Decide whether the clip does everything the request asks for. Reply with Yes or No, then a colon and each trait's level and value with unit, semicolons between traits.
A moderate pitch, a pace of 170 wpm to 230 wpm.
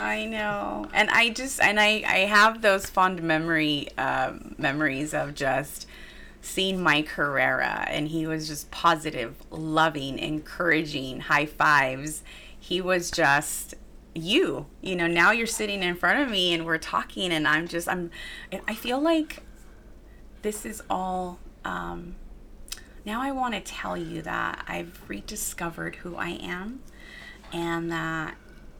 No: medium, 170 Hz; average, 145 wpm